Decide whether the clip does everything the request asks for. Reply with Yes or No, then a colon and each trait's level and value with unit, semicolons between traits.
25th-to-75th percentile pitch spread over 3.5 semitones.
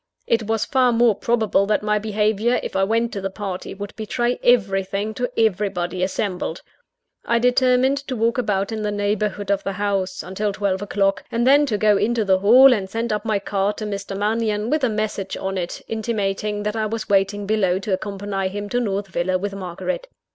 No: narrow, 2.5 semitones